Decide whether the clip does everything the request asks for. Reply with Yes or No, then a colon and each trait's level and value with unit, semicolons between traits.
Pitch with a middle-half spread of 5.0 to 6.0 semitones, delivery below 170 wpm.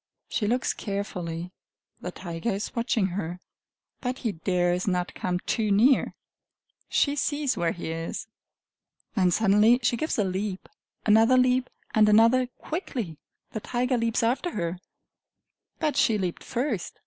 Yes: wide, 5.4 semitones; average, 140 wpm